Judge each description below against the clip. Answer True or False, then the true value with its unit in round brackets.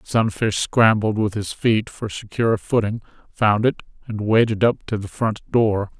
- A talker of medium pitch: False (110 Hz)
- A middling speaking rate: True (170 wpm)